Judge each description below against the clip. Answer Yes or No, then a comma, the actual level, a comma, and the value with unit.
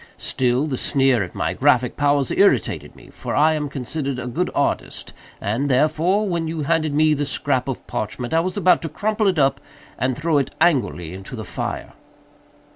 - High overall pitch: No, medium, 145 Hz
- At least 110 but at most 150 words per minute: No, average, 180 wpm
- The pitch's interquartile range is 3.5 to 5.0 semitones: Yes, average, 4.0 semitones